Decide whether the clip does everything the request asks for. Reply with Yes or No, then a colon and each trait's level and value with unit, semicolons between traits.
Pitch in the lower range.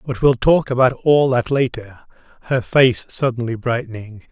Yes: low, 125 Hz